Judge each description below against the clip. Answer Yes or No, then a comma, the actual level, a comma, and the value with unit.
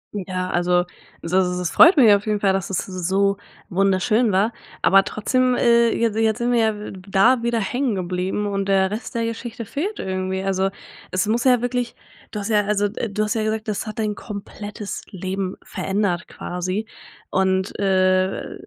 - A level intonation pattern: No, average, 3.0 semitones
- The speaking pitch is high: Yes, high, 205 Hz